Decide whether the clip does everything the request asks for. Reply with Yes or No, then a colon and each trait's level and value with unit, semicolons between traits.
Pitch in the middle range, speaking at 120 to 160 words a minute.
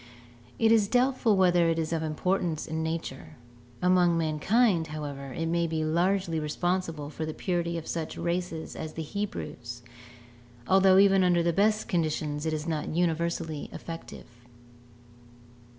Yes: medium, 165 Hz; average, 150 wpm